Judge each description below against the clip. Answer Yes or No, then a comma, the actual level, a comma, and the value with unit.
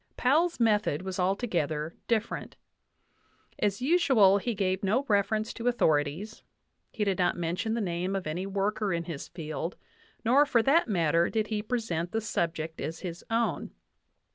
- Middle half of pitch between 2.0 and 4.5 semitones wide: No, average, 4.9 semitones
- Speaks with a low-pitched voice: No, high, 200 Hz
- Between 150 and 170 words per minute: Yes, average, 160 wpm